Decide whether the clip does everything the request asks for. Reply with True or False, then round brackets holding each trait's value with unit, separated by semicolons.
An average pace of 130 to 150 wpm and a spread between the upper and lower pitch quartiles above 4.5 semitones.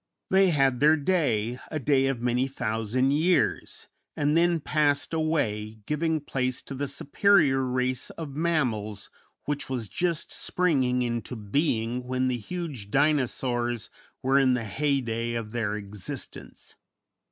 False (135 wpm; 4.2 semitones)